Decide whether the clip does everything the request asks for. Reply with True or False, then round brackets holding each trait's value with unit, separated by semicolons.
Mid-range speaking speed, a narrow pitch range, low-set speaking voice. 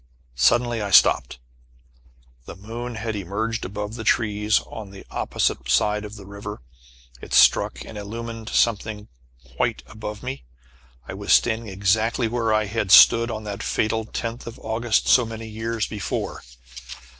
True (150 wpm; 1.8 semitones; 110 Hz)